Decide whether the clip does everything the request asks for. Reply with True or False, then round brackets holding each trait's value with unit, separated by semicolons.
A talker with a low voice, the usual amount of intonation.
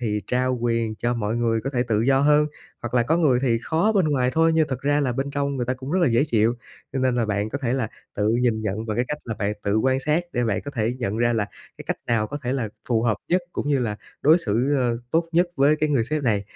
True (125 Hz; 4.0 semitones)